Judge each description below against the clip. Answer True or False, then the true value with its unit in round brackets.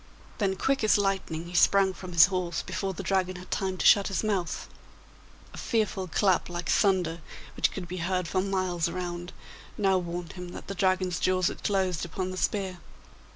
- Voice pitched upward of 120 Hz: True (185 Hz)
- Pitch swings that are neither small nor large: False (1.7 semitones)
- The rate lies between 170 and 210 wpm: True (190 wpm)